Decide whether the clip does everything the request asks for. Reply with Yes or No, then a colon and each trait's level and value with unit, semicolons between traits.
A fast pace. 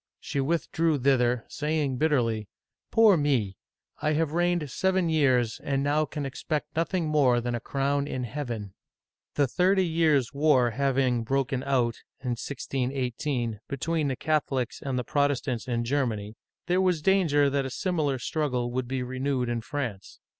No: average, 155 wpm